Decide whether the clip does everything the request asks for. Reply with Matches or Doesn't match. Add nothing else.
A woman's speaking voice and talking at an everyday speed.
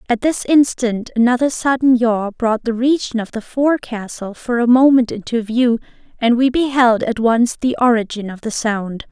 Matches